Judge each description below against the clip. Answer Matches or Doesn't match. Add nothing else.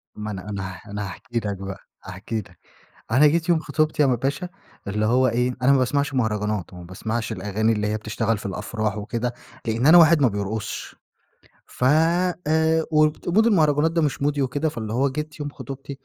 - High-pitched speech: Doesn't match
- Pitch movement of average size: Doesn't match